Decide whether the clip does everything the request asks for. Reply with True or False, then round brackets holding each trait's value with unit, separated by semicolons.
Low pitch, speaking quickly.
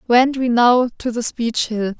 False (240 Hz; 210 wpm)